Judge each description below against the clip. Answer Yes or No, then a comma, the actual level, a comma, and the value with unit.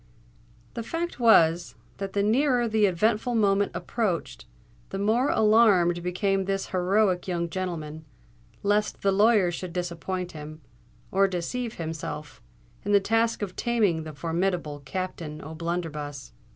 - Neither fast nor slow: No, slow, 130 wpm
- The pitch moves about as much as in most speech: Yes, average, 4.0 semitones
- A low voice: No, medium, 185 Hz